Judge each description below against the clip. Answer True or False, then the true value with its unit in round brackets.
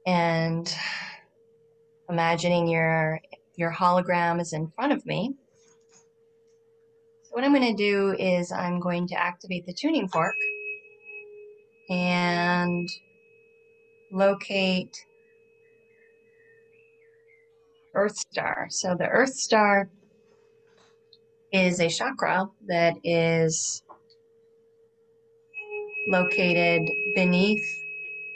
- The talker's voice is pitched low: False (255 Hz)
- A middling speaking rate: False (85 wpm)